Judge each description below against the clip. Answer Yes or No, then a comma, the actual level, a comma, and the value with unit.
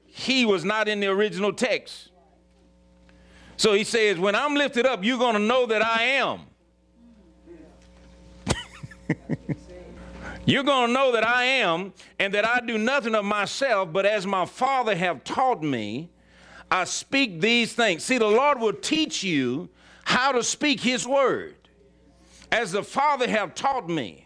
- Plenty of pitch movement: Yes, wide, 6.6 semitones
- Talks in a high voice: Yes, high, 215 Hz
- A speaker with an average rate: Yes, average, 155 wpm